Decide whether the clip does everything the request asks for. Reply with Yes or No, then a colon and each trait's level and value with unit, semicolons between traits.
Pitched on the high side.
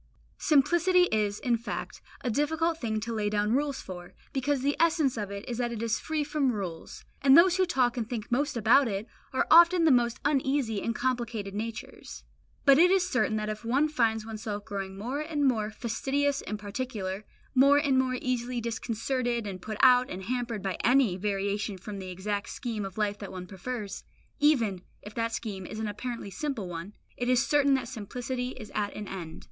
Yes: high, 235 Hz